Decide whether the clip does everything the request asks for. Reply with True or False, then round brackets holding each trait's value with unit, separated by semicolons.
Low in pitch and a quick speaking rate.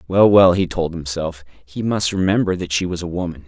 True (90 Hz; 225 wpm)